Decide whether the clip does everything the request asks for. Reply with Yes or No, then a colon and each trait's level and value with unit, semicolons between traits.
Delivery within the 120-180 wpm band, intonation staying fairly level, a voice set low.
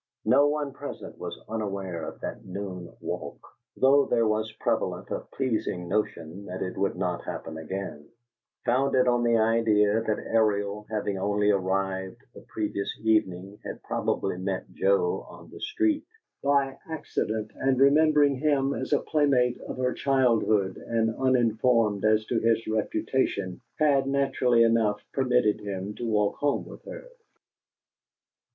No: average, 145 wpm; average, 4.9 semitones; low, 110 Hz